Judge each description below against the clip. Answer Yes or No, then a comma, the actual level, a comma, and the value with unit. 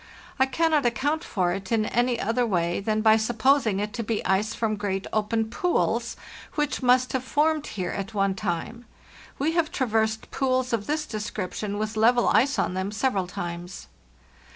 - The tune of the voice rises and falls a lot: No, average, 4.2 semitones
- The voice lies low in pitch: No, high, 220 Hz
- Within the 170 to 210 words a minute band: Yes, average, 175 wpm